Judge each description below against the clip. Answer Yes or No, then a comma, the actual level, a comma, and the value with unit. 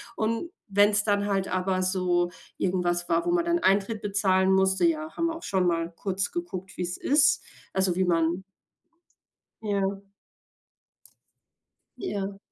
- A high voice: Yes, high, 195 Hz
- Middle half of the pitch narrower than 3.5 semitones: Yes, narrow, 2.4 semitones